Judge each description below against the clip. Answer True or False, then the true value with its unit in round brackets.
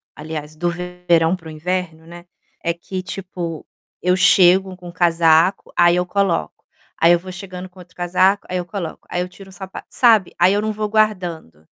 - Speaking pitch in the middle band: True (180 Hz)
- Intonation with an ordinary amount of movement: False (1.9 semitones)